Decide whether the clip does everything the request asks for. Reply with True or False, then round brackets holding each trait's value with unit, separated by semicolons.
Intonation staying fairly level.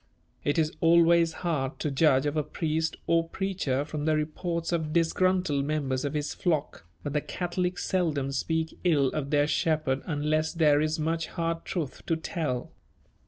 True (2.3 semitones)